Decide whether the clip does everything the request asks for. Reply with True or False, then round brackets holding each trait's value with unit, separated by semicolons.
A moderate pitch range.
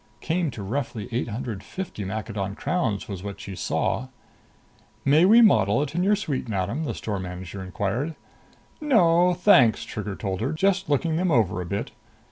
False (8.8 semitones)